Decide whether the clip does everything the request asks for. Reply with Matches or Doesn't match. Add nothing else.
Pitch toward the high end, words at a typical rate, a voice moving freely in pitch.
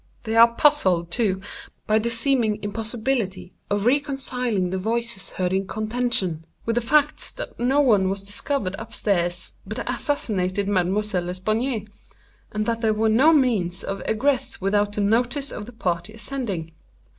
Doesn't match